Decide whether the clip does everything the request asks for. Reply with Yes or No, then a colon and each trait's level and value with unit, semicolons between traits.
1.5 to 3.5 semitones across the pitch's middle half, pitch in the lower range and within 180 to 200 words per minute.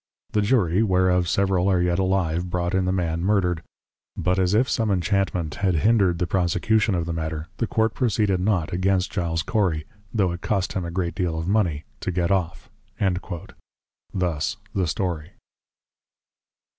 No: narrow, 2.4 semitones; very low, 90 Hz; average, 165 wpm